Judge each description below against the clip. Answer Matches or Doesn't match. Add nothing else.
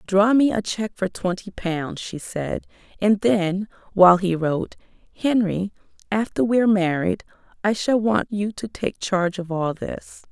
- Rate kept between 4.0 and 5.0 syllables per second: Matches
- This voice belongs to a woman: Matches